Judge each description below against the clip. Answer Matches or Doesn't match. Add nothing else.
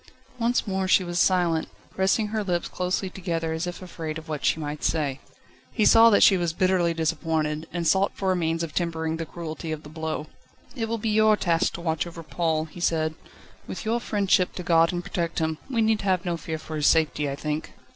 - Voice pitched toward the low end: Doesn't match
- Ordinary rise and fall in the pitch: Matches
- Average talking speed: Doesn't match